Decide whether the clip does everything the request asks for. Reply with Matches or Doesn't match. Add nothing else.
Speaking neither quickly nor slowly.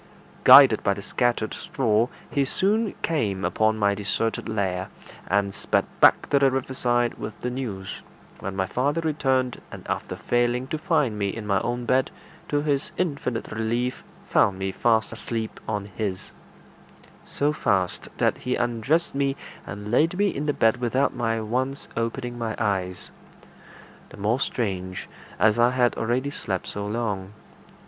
Matches